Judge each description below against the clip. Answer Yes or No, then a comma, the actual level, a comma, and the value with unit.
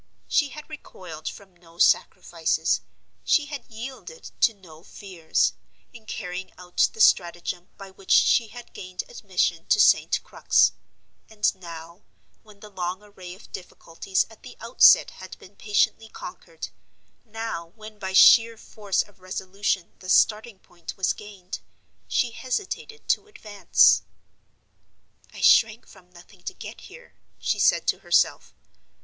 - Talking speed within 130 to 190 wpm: Yes, average, 140 wpm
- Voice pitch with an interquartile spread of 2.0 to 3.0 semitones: No, average, 3.7 semitones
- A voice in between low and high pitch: No, high, 200 Hz